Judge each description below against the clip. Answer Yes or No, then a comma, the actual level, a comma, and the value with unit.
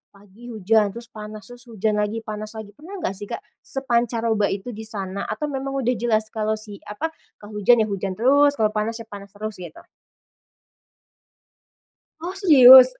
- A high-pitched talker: Yes, high, 220 Hz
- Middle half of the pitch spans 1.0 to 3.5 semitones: Yes, average, 2.7 semitones